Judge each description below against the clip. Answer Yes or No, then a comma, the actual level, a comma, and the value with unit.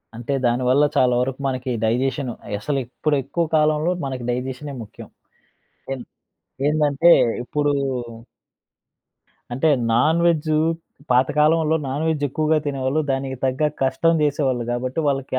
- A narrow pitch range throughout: No, average, 3.0 semitones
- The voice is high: No, low, 135 Hz